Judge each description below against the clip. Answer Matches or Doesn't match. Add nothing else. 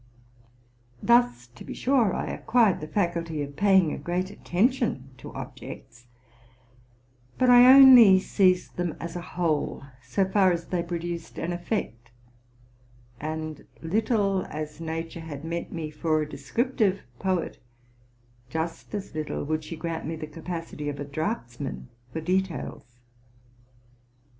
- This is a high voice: Doesn't match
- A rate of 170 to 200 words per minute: Doesn't match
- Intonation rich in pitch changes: Doesn't match